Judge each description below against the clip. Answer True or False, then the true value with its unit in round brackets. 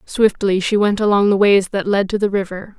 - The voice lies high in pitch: True (200 Hz)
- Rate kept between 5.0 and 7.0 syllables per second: True (5.2 syllables/s)